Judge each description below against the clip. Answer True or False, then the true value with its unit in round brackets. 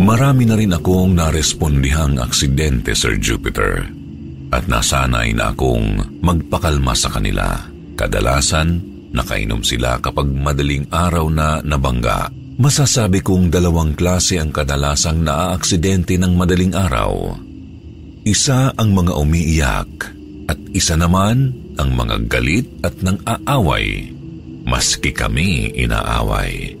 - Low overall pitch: True (85 Hz)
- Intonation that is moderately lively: True (4.7 semitones)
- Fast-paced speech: False (110 wpm)